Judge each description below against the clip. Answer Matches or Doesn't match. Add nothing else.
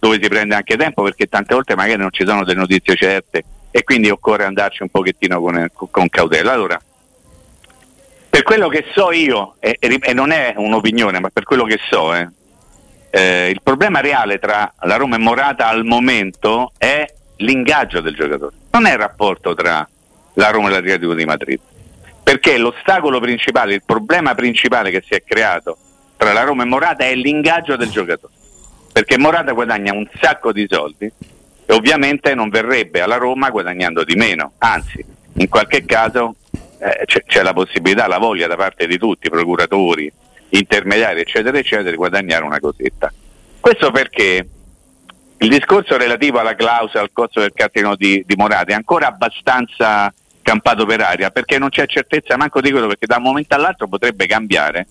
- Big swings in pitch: Matches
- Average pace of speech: Doesn't match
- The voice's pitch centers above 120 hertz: Doesn't match